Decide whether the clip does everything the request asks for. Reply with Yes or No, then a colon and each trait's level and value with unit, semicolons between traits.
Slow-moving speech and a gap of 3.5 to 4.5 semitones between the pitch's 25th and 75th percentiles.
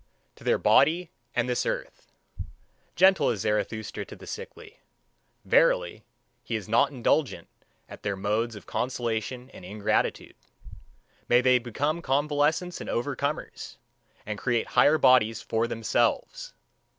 No: slow, 125 wpm; average, 5.3 semitones